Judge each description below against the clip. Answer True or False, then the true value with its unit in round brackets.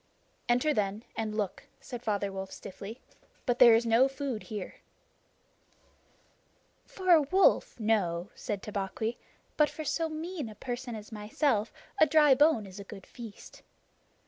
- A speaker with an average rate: True (145 wpm)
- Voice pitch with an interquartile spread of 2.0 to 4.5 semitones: False (5.2 semitones)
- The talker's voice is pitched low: False (225 Hz)